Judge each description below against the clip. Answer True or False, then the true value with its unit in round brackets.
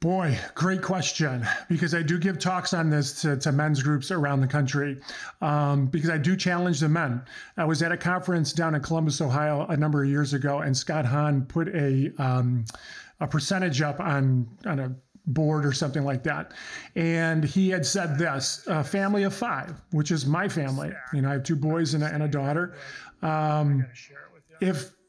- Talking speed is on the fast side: False (195 wpm)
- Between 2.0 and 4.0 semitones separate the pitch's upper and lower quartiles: True (3.2 semitones)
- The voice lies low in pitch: False (155 Hz)